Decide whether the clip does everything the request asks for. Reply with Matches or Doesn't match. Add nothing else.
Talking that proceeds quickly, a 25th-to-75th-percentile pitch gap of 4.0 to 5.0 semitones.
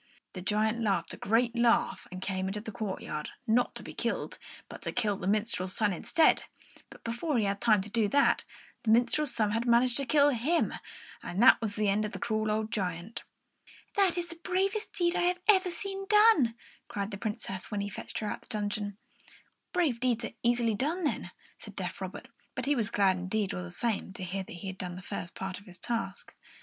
Matches